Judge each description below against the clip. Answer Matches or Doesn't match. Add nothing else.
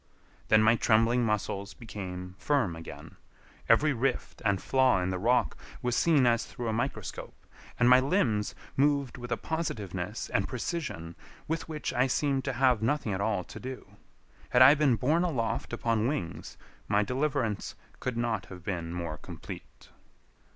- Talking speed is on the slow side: Doesn't match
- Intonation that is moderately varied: Matches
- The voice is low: Matches